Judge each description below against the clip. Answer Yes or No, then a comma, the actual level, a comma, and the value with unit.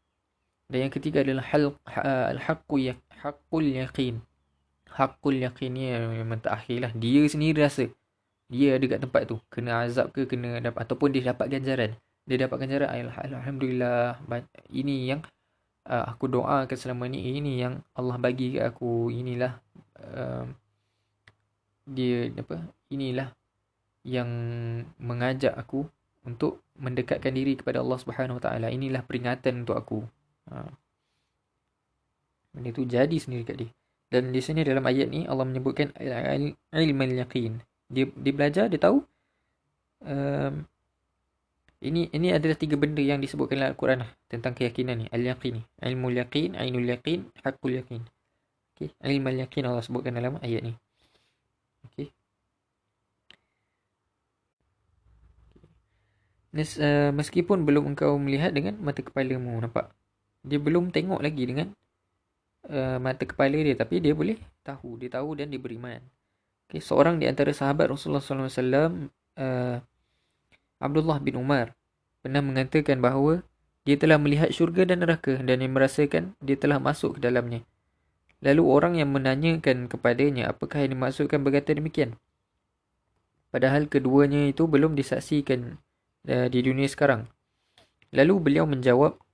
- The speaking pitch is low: Yes, low, 130 Hz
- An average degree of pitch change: Yes, average, 3.1 semitones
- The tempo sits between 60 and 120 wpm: No, average, 135 wpm